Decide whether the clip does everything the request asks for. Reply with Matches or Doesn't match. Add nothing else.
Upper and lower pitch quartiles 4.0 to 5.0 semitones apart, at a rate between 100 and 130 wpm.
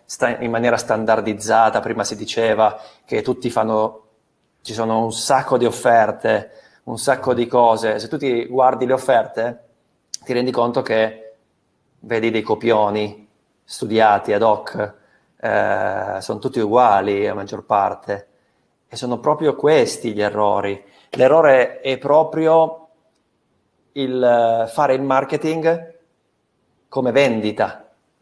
Doesn't match